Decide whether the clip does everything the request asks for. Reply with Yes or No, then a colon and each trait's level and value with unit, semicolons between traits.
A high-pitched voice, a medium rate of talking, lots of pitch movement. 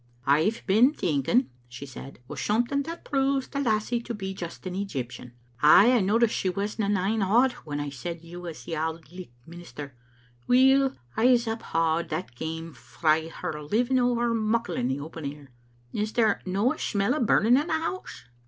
Yes: high, 195 Hz; average, 180 wpm; wide, 7.0 semitones